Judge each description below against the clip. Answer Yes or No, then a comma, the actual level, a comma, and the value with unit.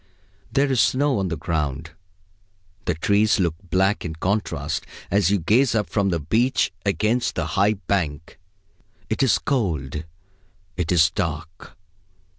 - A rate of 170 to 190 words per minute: No, average, 140 wpm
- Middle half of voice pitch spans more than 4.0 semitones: Yes, average, 4.8 semitones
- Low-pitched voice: Yes, very low, 95 Hz